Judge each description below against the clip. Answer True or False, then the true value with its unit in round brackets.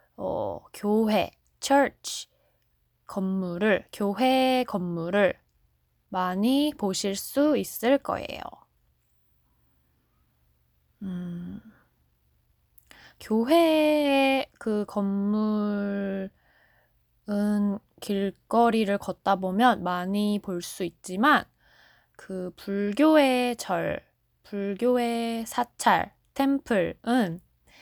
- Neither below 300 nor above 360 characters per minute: False (135 characters per minute)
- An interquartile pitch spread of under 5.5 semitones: True (5.1 semitones)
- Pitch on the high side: True (200 Hz)